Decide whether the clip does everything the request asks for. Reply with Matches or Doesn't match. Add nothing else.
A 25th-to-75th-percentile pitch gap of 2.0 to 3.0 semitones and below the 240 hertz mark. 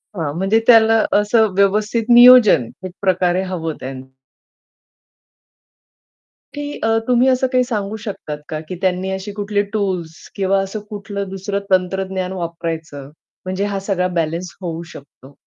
Doesn't match